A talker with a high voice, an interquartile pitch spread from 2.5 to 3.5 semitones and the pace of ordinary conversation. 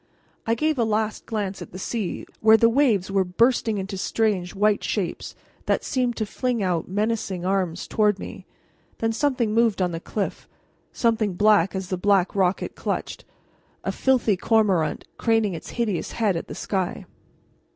Yes: high, 210 Hz; average, 3.2 semitones; average, 170 wpm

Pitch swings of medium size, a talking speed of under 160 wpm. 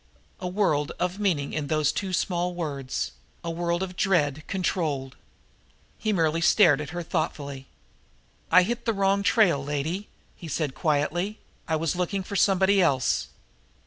Yes: average, 4.3 semitones; average, 150 wpm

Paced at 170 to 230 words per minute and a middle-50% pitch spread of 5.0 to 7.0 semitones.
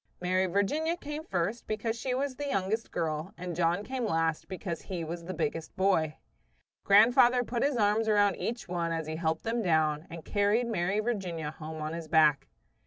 Yes: average, 185 wpm; wide, 5.6 semitones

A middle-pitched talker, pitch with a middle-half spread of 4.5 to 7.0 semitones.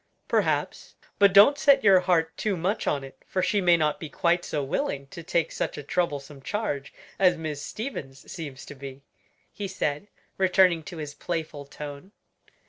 Yes: medium, 165 Hz; average, 4.8 semitones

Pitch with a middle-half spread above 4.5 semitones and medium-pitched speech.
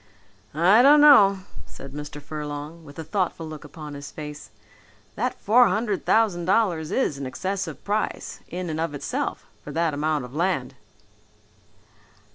Yes: average, 5.1 semitones; medium, 165 Hz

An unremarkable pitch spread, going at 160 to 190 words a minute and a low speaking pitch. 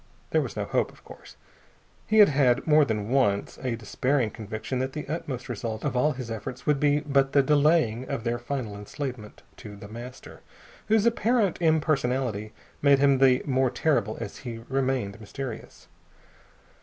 Yes: average, 4.0 semitones; average, 170 wpm; low, 130 Hz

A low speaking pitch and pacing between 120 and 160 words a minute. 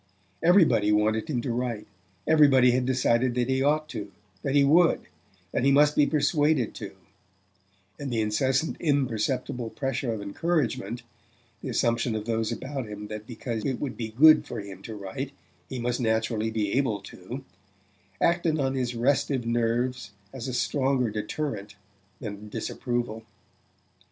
Yes: low, 120 Hz; average, 150 wpm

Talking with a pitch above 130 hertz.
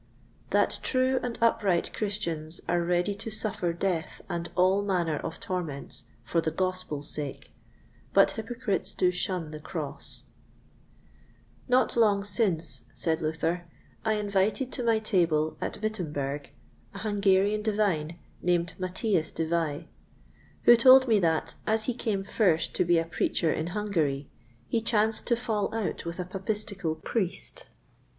Yes: medium, 185 Hz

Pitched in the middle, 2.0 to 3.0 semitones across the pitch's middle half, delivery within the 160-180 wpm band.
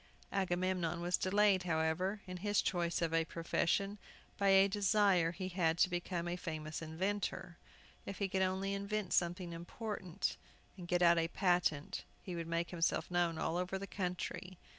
Yes: medium, 180 Hz; narrow, 2.4 semitones; average, 165 wpm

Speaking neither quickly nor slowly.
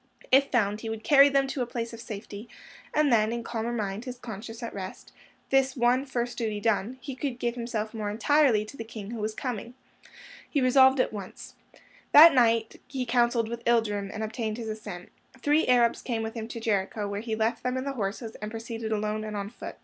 No: fast, 215 wpm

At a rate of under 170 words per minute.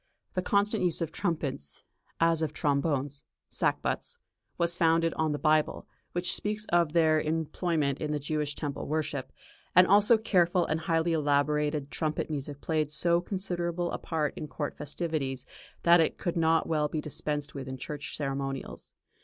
Yes: average, 160 wpm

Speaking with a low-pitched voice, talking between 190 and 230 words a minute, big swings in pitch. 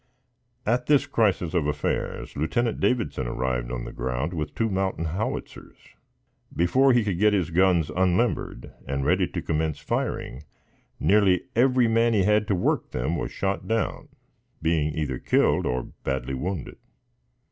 No: very low, 90 Hz; average, 150 wpm; wide, 6.6 semitones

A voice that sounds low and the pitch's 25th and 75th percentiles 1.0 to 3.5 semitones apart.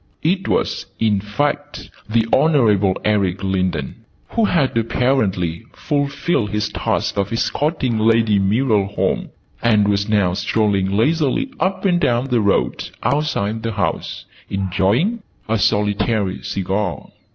No: low, 110 Hz; wide, 5.4 semitones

